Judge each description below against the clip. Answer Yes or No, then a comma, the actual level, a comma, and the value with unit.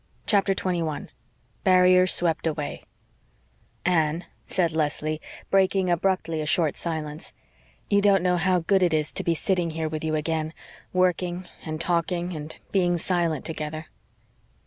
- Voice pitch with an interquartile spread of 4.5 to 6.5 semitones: No, average, 2.7 semitones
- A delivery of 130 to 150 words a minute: Yes, average, 140 wpm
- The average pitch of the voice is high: No, medium, 170 Hz